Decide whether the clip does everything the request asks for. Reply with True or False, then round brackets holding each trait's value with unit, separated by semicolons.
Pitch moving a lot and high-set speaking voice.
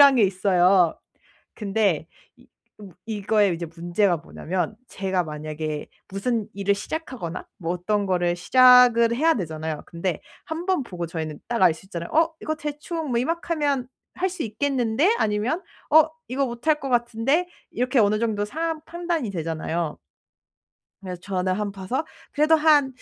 True (7.8 semitones; 215 Hz)